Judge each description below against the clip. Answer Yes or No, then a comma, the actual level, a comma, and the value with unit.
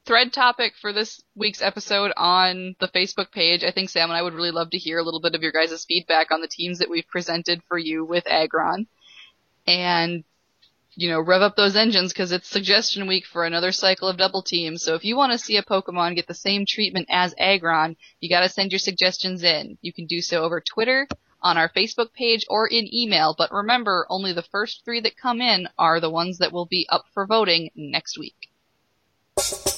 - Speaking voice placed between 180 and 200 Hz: Yes, medium, 185 Hz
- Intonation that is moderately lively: Yes, average, 3.3 semitones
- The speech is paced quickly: Yes, fast, 215 wpm